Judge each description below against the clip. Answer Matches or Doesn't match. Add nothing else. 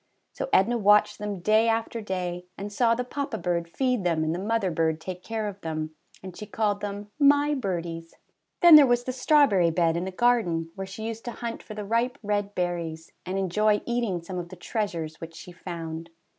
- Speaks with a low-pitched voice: Doesn't match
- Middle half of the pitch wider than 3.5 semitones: Matches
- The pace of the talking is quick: Matches